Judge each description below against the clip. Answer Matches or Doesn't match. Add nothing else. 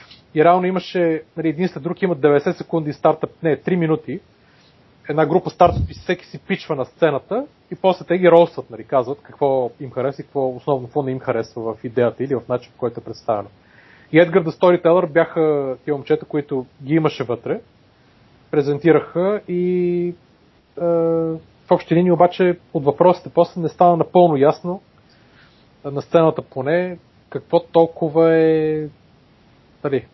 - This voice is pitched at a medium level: Matches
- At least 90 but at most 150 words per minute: Doesn't match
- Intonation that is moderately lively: Matches